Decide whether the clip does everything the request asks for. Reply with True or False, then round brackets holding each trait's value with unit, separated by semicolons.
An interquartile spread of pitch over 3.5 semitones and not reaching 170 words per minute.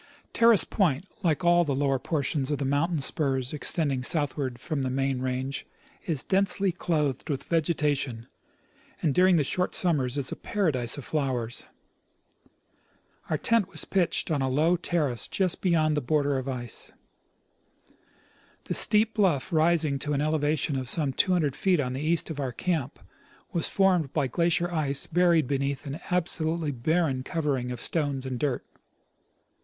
True (4.2 semitones; 160 wpm)